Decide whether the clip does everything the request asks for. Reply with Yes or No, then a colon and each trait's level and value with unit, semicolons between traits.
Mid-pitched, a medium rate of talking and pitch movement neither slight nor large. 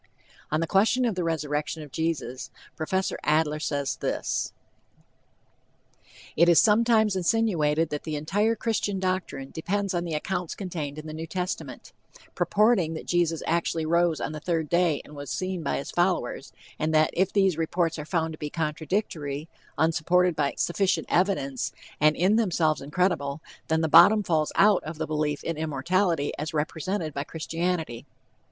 Yes: medium, 165 Hz; average, 160 wpm; average, 3.3 semitones